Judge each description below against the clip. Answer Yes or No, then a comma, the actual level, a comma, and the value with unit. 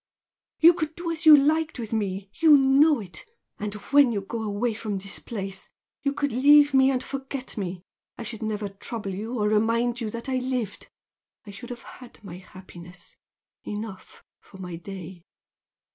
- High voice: Yes, high, 225 Hz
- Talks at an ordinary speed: Yes, average, 175 wpm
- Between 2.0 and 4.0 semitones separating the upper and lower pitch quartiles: No, average, 5.3 semitones